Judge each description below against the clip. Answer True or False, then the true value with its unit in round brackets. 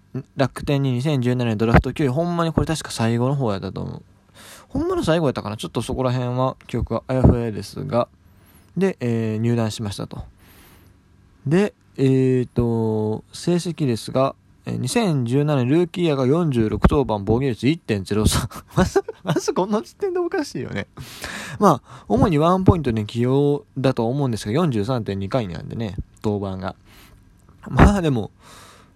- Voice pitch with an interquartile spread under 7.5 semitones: True (5.3 semitones)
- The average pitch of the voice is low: True (125 Hz)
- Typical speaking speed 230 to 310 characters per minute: True (290 characters per minute)